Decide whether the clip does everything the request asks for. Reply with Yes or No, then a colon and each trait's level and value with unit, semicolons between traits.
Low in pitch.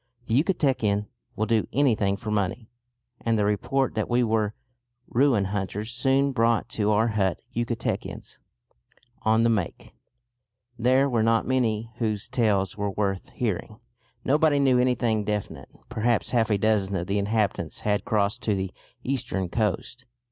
Yes: low, 110 Hz